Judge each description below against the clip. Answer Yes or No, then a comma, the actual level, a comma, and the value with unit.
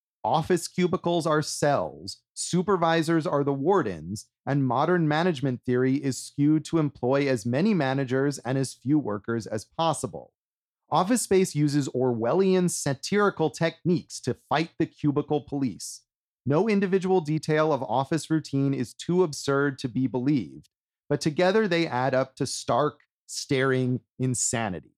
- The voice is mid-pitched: Yes, medium, 145 Hz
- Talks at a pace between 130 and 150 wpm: Yes, slow, 135 wpm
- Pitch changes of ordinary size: Yes, average, 4.2 semitones